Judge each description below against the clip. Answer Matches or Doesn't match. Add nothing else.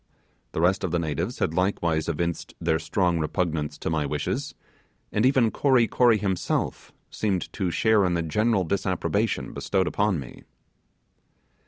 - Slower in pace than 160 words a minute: Matches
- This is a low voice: Matches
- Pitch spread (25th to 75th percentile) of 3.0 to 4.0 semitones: Doesn't match